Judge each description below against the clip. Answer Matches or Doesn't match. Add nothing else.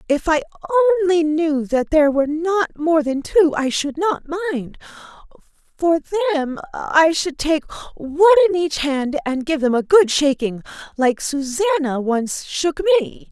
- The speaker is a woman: Matches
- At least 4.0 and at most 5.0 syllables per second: Matches